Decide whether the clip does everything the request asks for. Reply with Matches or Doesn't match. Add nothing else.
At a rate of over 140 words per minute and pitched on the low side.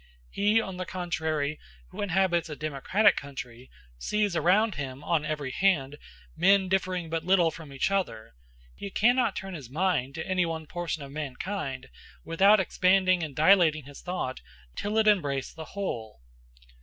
Doesn't match